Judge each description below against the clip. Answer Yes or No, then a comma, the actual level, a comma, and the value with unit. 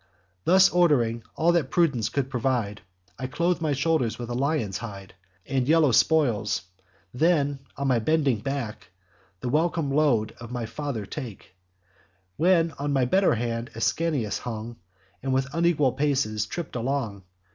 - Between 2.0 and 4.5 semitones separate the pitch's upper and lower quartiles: No, average, 5.0 semitones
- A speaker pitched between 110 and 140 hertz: Yes, low, 135 Hz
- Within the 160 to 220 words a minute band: No, average, 150 wpm